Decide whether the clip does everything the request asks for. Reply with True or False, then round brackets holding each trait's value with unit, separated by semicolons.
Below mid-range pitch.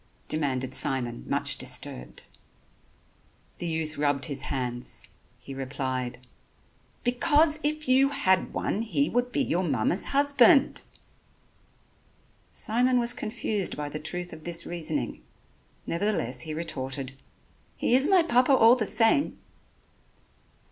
False (175 Hz)